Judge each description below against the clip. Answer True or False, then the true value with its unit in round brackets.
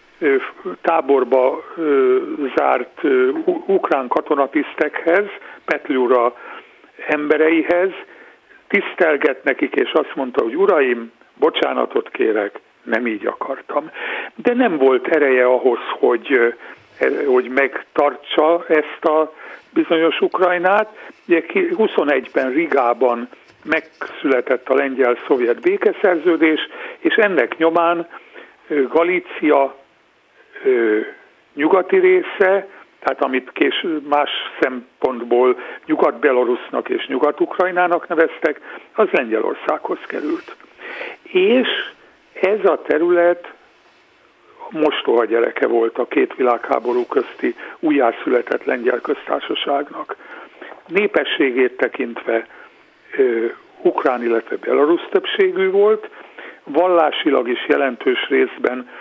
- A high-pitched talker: True (350 Hz)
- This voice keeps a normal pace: False (80 wpm)